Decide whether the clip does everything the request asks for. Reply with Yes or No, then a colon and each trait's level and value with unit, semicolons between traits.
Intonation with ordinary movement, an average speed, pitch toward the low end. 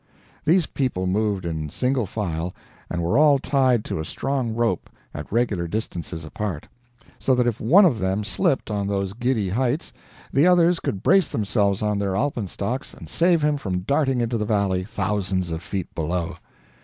No: wide, 6.0 semitones; average, 175 wpm; low, 105 Hz